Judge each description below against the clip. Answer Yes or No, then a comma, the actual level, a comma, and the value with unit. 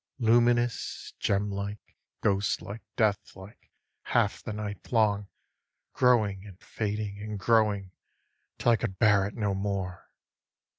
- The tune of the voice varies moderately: No, narrow, 1.8 semitones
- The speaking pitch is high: No, low, 105 Hz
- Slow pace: Yes, slow, 110 wpm